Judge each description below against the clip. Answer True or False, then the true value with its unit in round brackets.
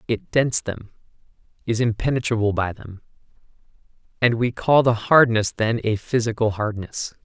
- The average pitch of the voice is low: True (115 Hz)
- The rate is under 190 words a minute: True (135 wpm)